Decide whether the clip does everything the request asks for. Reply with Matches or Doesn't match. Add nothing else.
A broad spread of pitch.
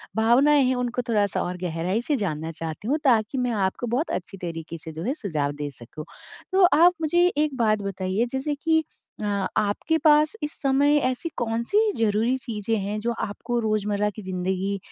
Matches